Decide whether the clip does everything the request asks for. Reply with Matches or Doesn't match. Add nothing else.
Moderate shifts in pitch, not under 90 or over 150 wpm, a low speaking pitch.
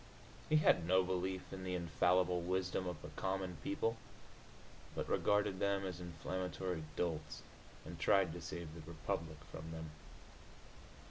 Doesn't match